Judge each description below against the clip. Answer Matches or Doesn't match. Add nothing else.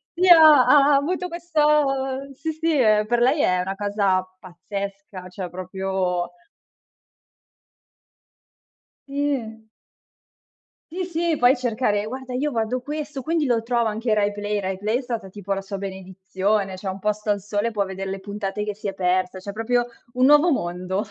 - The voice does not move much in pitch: Doesn't match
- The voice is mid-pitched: Doesn't match